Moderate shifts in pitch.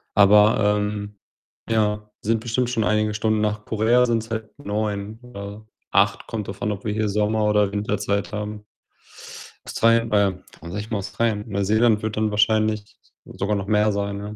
No: narrow, 1.1 semitones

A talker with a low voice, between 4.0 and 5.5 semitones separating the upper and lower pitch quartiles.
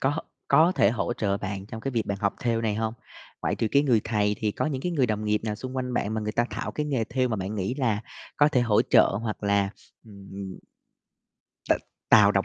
No: low, 110 Hz; average, 3.6 semitones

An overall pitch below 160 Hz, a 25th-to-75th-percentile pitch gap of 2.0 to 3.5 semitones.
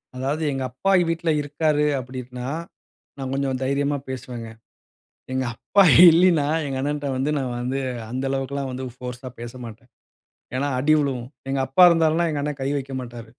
Yes: low, 135 Hz; narrow, 2.4 semitones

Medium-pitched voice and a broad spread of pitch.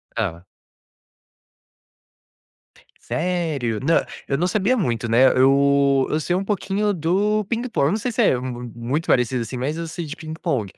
Yes: medium, 150 Hz; wide, 6.7 semitones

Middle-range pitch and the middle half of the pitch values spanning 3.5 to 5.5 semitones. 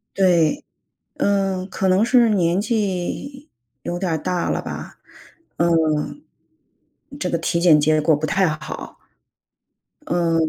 No: medium, 180 Hz; average, 3.0 semitones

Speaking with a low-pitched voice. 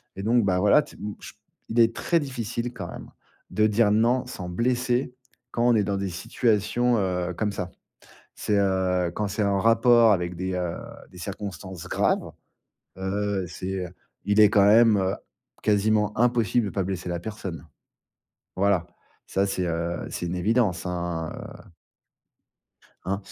Yes: low, 100 Hz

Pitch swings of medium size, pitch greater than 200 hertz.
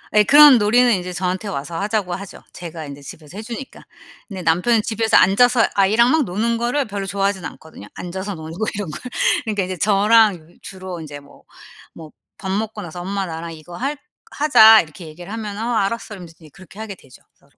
No: average, 4.2 semitones; high, 195 Hz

